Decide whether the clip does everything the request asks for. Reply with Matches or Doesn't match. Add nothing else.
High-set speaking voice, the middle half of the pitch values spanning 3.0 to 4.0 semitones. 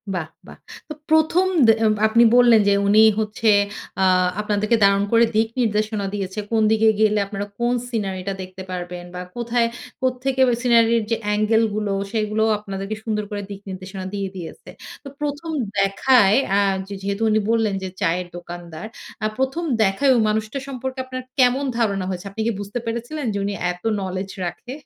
Matches